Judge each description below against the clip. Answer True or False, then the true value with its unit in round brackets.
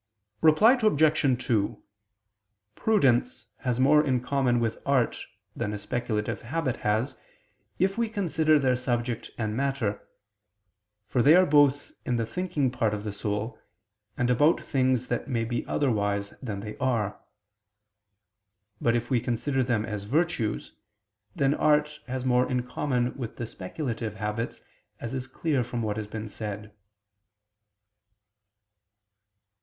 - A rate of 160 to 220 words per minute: False (140 wpm)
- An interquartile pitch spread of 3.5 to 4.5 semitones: True (4.2 semitones)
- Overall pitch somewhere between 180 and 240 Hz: False (125 Hz)